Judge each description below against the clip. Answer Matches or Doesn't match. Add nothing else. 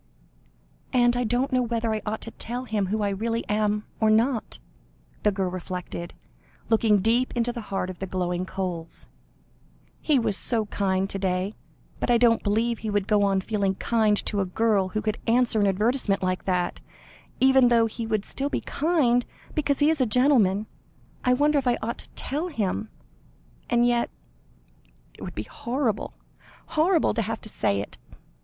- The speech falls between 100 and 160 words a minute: Doesn't match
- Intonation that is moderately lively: Matches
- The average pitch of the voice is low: Doesn't match